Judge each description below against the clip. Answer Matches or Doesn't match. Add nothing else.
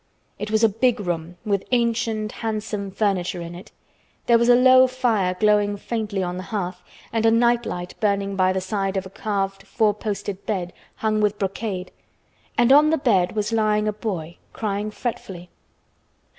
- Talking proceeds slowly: Doesn't match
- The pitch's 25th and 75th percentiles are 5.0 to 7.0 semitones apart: Doesn't match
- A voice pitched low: Doesn't match